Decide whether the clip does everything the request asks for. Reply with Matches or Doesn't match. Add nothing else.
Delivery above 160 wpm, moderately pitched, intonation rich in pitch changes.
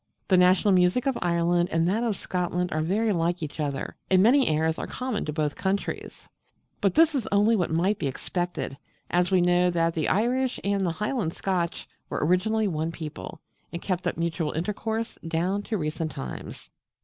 Doesn't match